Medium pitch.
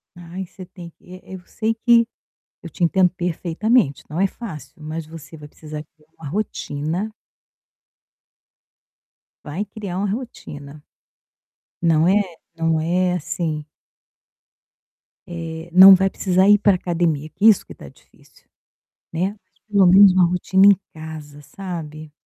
Yes: medium, 175 Hz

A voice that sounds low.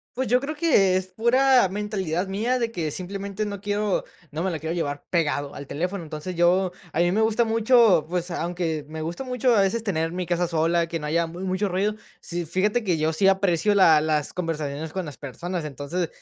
No: medium, 180 Hz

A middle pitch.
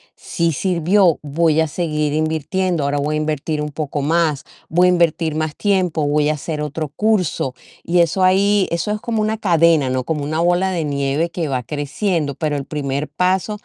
Yes: medium, 160 Hz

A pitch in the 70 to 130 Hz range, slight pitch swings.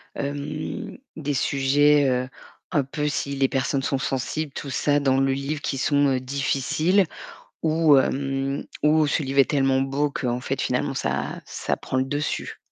No: medium, 140 Hz; narrow, 1.6 semitones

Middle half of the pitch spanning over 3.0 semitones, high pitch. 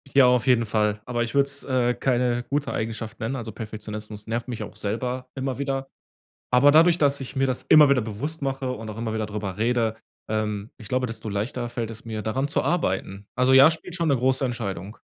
No: average, 3.6 semitones; low, 120 Hz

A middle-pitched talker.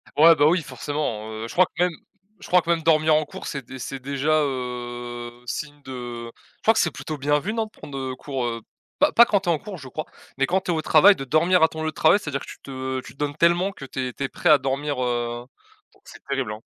Yes: medium, 145 Hz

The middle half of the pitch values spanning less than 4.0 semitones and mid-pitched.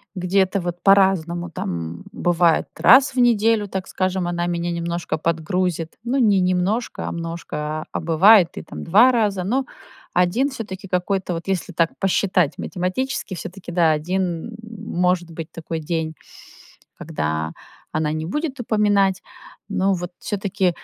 Yes: average, 3.1 semitones; medium, 180 Hz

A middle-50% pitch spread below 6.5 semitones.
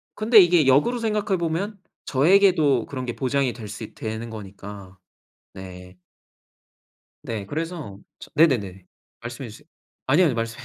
No: wide, 7.8 semitones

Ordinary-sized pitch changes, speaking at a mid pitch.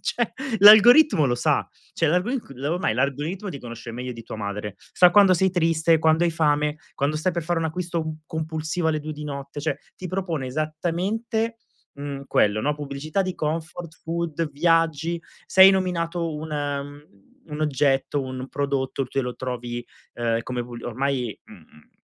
Yes: average, 3.7 semitones; medium, 155 Hz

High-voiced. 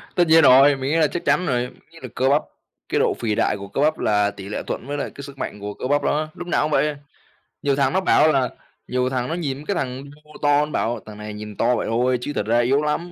No: low, 135 Hz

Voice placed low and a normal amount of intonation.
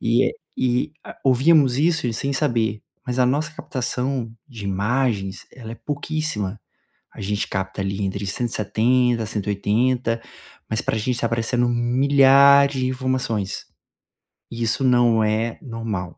Yes: low, 120 Hz; average, 3.3 semitones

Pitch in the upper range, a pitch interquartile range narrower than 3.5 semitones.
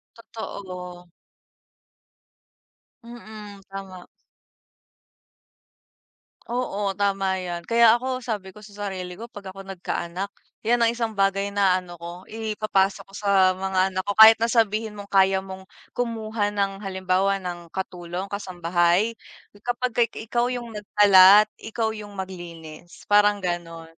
Yes: high, 195 Hz; average, 2.7 semitones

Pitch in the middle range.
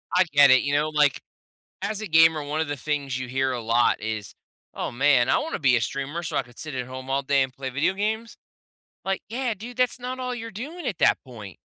Yes: medium, 145 Hz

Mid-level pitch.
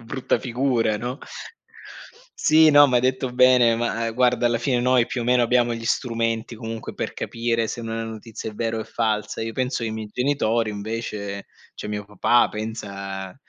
No: low, 115 Hz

